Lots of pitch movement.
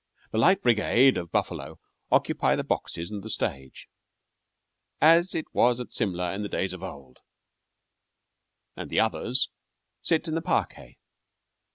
Yes: wide, 7.2 semitones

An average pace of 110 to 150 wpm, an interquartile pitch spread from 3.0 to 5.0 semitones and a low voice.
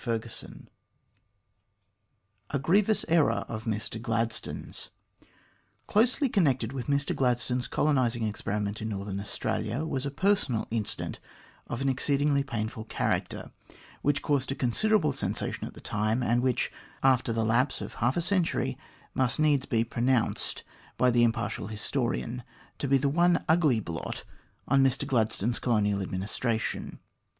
Yes: average, 140 wpm; average, 4.0 semitones; low, 125 Hz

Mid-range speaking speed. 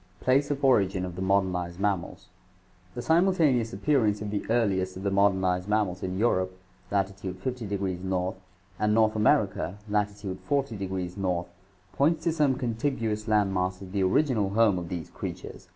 Yes: average, 170 wpm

